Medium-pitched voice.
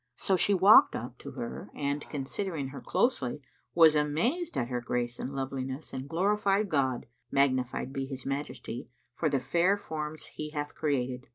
Yes: medium, 145 Hz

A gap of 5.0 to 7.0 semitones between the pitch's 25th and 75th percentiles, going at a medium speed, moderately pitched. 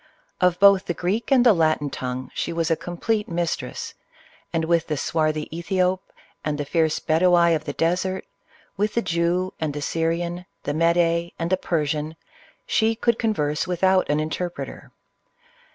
No: average, 2.8 semitones; average, 165 wpm; medium, 170 Hz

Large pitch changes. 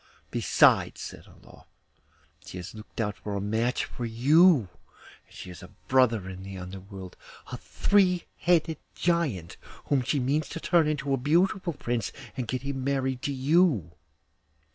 Yes: wide, 7.2 semitones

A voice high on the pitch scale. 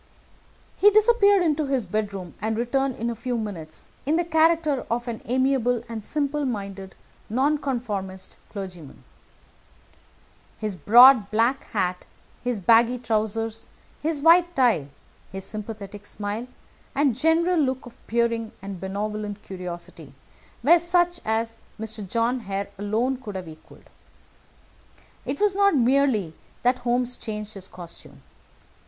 Yes: high, 230 Hz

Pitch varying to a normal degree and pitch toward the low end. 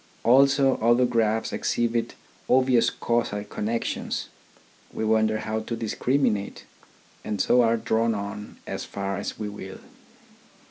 No: narrow, 2.0 semitones; low, 115 Hz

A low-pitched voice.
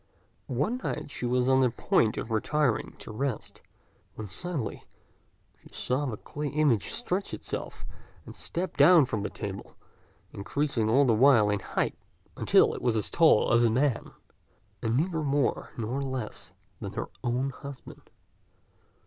Yes: low, 130 Hz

